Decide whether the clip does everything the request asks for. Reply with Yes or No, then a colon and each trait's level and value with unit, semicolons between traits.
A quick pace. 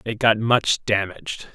No: average, 155 wpm